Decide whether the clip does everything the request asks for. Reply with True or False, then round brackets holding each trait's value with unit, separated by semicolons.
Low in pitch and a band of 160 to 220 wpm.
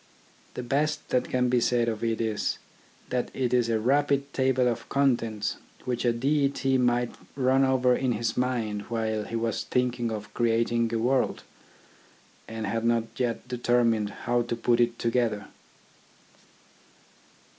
False (120 Hz; 150 wpm)